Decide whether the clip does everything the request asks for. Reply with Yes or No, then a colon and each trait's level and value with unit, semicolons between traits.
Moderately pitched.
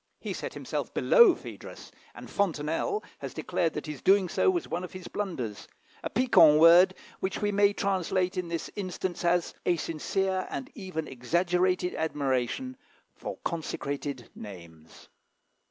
Yes: medium, 180 Hz